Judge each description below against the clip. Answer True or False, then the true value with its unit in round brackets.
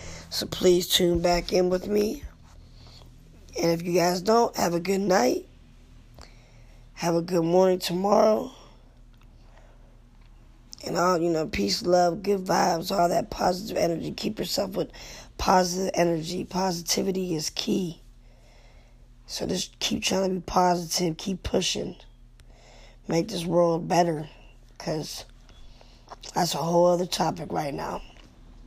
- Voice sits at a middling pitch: True (175 Hz)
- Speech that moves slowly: True (130 wpm)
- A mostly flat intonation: True (1.6 semitones)